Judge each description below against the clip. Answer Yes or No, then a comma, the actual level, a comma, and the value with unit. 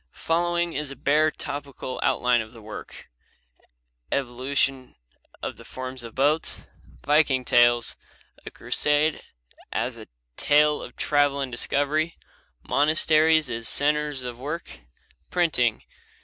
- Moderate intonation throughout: Yes, average, 3.2 semitones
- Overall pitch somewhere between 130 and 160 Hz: Yes, medium, 140 Hz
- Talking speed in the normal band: No, slow, 120 wpm